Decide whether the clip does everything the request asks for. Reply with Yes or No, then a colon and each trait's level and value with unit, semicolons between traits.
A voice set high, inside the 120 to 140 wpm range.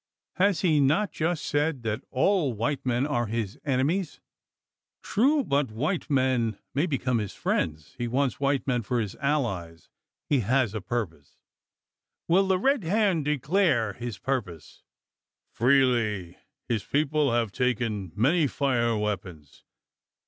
No: low, 130 Hz; slow, 135 wpm